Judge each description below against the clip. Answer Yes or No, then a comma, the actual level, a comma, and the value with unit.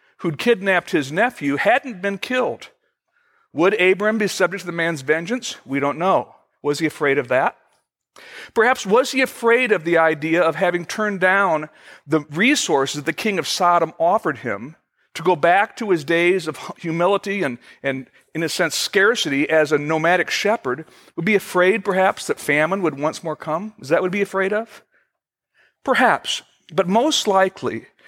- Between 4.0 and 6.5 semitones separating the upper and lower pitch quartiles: Yes, average, 4.4 semitones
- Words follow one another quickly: No, average, 175 wpm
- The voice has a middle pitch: Yes, medium, 180 Hz